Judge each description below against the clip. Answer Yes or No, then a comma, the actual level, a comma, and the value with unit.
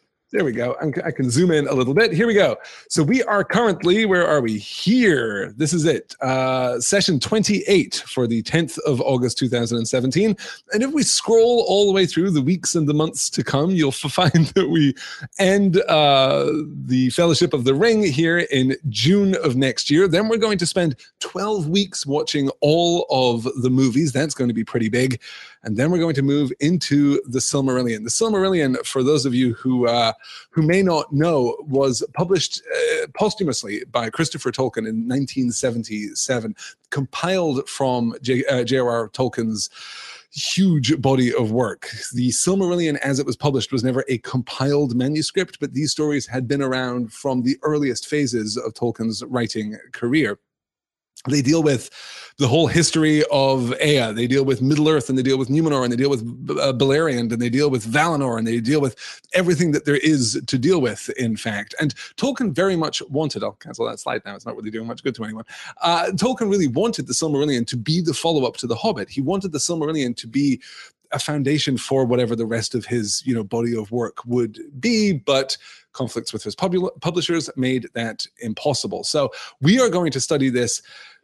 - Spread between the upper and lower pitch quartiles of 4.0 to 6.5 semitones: Yes, average, 5.1 semitones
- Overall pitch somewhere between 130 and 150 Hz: Yes, medium, 140 Hz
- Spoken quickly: No, average, 190 wpm